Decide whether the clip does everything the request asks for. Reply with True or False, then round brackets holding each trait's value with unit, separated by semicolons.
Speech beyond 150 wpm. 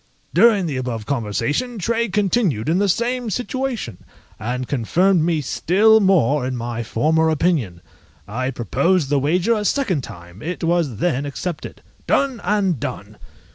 False (145 wpm)